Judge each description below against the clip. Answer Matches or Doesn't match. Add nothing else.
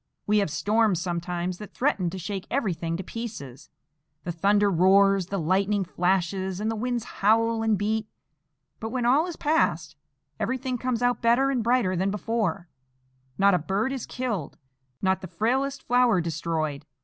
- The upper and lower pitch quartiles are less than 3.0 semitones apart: Doesn't match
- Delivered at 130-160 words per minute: Matches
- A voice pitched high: Matches